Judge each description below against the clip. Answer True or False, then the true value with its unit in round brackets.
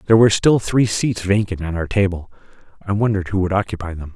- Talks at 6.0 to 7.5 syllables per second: True (6.6 syllables/s)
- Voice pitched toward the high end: False (100 Hz)